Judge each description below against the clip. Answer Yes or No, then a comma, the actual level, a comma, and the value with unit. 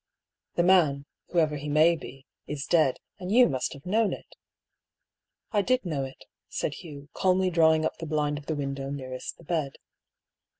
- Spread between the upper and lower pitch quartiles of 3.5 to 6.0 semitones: Yes, average, 4.0 semitones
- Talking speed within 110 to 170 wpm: No, average, 185 wpm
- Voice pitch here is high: No, medium, 155 Hz